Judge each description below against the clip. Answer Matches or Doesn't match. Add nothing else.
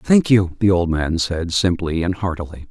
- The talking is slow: Doesn't match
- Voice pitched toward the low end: Matches